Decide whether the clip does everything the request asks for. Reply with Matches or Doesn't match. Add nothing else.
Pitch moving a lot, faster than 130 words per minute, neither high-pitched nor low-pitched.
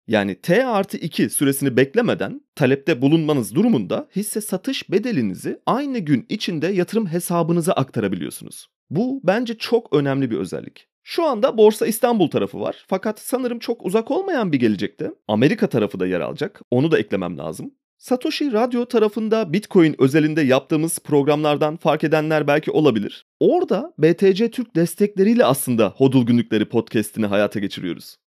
Matches